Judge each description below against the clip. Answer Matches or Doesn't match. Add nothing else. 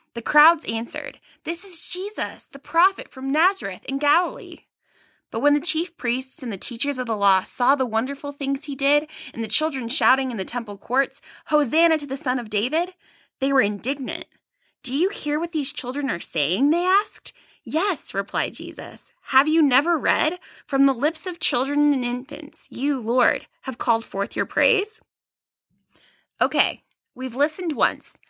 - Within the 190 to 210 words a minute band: Doesn't match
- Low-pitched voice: Doesn't match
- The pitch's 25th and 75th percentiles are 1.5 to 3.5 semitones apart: Doesn't match